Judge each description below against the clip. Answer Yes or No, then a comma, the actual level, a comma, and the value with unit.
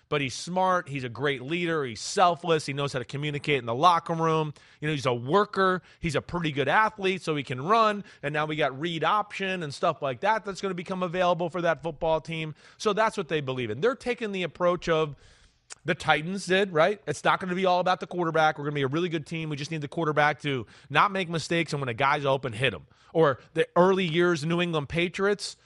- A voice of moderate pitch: Yes, medium, 165 Hz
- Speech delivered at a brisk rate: Yes, fast, 250 wpm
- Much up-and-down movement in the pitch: No, average, 3.8 semitones